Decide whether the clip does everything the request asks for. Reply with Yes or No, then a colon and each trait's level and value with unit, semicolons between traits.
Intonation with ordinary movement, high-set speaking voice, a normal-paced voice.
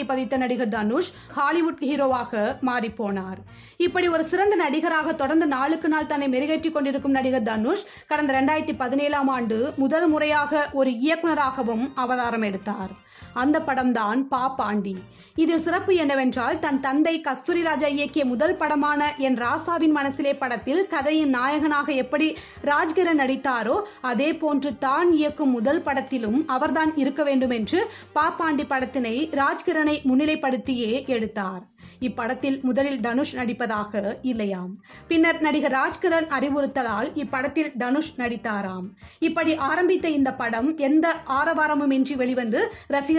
Yes: average, 3.3 semitones; very high, 280 Hz; average, 120 wpm